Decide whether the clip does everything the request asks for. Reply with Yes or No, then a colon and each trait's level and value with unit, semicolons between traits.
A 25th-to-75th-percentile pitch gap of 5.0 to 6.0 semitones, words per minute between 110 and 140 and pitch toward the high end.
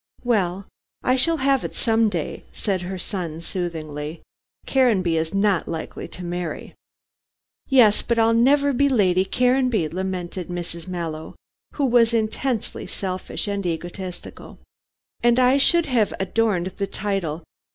Yes: wide, 5.4 semitones; slow, 135 wpm; high, 195 Hz